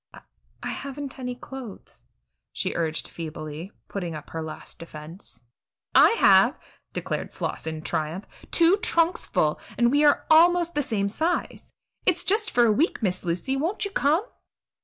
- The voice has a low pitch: No, high, 245 Hz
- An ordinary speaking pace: Yes, average, 160 wpm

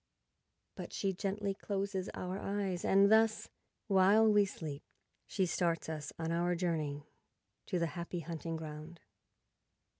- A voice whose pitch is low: No, medium, 180 Hz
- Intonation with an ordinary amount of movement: Yes, average, 3.3 semitones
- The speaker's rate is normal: No, slow, 130 wpm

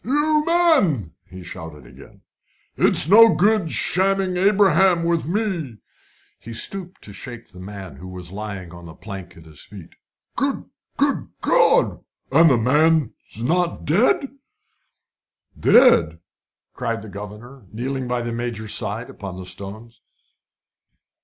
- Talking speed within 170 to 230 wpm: No, slow, 135 wpm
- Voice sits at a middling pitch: No, low, 120 Hz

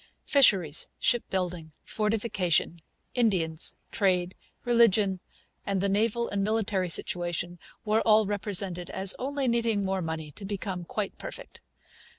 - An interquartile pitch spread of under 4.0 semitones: Yes, average, 3.6 semitones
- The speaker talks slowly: Yes, slow, 115 wpm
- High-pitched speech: Yes, high, 195 Hz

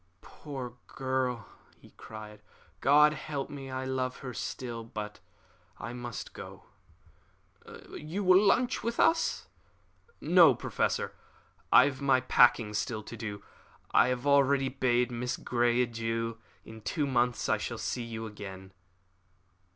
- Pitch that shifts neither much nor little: Yes, average, 3.1 semitones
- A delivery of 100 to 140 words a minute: Yes, slow, 135 wpm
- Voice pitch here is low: Yes, low, 125 Hz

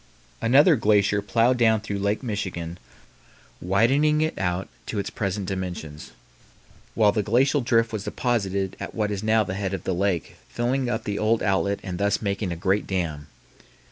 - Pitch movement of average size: Yes, average, 3.1 semitones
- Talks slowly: No, average, 170 wpm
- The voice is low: Yes, low, 100 Hz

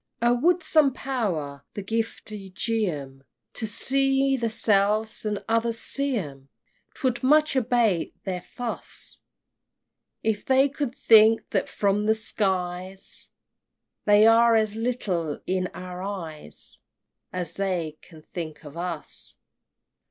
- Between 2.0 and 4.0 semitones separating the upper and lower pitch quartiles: No, average, 4.7 semitones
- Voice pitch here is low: No, high, 215 Hz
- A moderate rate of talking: No, slow, 125 wpm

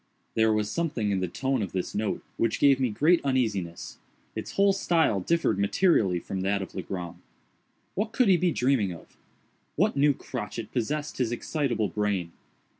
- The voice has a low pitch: Yes, low, 115 Hz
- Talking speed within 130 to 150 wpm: No, average, 170 wpm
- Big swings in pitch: Yes, wide, 6.9 semitones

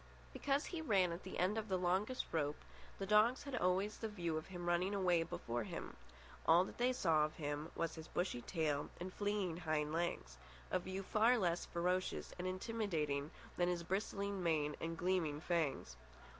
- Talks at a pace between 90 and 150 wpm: No, average, 180 wpm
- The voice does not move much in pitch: No, average, 3.7 semitones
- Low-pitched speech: No, medium, 175 Hz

